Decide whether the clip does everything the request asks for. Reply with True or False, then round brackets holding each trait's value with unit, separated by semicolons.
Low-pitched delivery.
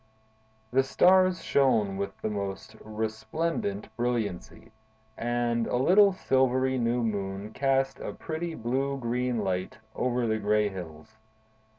True (120 Hz)